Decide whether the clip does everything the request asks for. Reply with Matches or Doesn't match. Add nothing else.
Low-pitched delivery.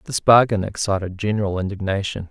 Matches